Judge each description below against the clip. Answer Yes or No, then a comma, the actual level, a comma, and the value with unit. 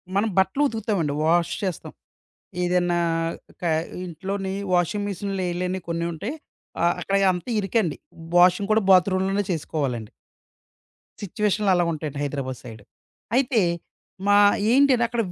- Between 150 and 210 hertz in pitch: Yes, medium, 185 Hz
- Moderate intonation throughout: Yes, average, 3.4 semitones